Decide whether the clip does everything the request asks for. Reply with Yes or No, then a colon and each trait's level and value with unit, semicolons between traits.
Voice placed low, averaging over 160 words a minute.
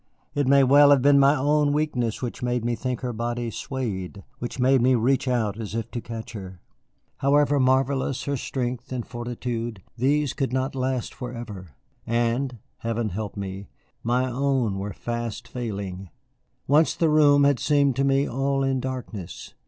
Yes: low, 125 Hz; average, 170 wpm